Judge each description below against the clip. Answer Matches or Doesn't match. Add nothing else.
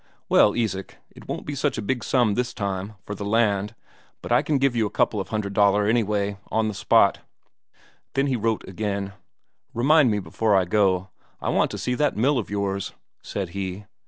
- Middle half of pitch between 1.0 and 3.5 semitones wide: Matches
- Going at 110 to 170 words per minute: Doesn't match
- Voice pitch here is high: Doesn't match